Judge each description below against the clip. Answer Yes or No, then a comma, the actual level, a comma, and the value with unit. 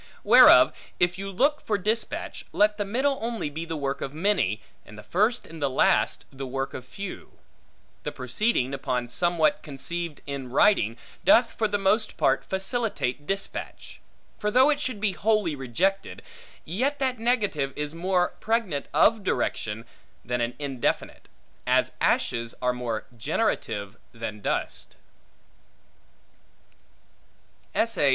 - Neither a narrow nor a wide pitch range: No, wide, 8.4 semitones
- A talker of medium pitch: Yes, medium, 175 Hz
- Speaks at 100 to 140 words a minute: Yes, slow, 135 wpm